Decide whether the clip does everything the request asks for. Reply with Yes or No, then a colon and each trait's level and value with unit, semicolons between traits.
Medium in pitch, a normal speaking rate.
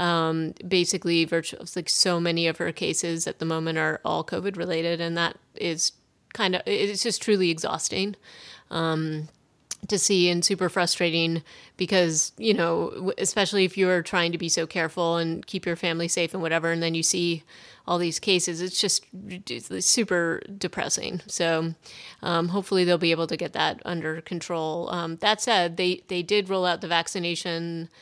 Yes: medium, 175 Hz; average, 175 wpm